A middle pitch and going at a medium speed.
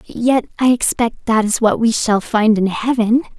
No: high, 230 Hz; average, 195 wpm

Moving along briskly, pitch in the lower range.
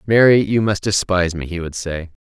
Yes: fast, 215 wpm; very low, 95 Hz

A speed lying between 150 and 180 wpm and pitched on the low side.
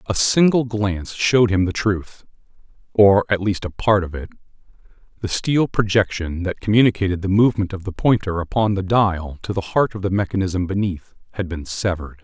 Yes: average, 175 wpm; low, 100 Hz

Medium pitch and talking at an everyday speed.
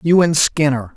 Yes: medium, 150 Hz; average, 190 wpm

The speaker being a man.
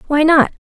No: female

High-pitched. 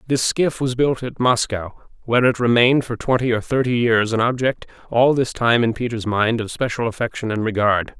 No: low, 120 Hz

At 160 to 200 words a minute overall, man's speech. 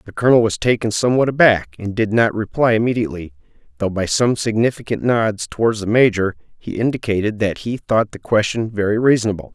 Yes: average, 175 wpm; male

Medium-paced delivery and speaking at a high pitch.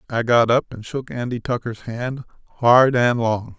No: average, 185 wpm; low, 120 Hz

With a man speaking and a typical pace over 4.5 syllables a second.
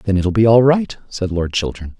Yes: male; 4.8 syllables/s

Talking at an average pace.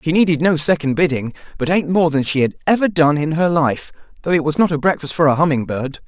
No: fast, 255 wpm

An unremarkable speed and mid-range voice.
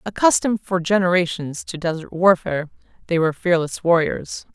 No: slow, 130 wpm; medium, 175 Hz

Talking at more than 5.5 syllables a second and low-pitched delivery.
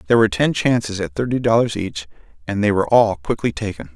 Yes: 6.5 syllables/s; low, 100 Hz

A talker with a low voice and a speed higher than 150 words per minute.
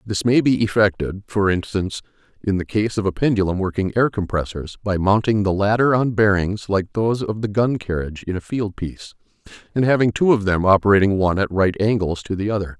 Yes: low, 100 Hz; fast, 205 wpm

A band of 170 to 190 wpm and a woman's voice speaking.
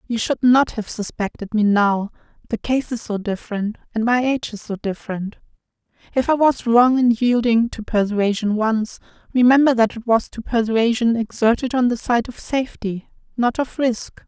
Yes: average, 175 wpm; female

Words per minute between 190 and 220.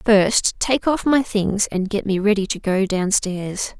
Yes: fast, 205 wpm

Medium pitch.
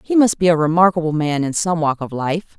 Yes: medium, 165 Hz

